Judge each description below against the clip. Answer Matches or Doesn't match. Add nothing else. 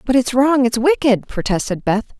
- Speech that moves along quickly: Doesn't match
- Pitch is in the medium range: Doesn't match